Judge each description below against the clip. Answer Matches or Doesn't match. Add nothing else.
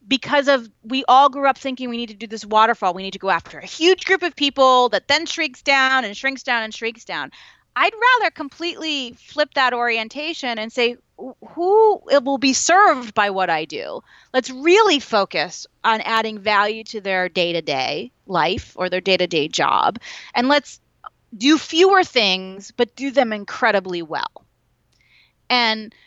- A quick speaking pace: Doesn't match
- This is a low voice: Doesn't match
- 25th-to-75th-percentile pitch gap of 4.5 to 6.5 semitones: Matches